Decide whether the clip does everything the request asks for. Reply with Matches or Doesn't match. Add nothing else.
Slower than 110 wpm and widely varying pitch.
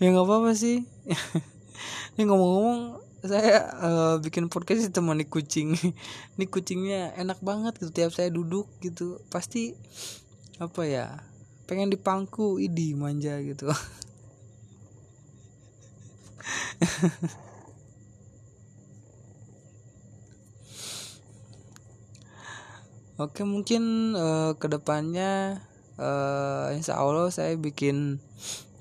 Matches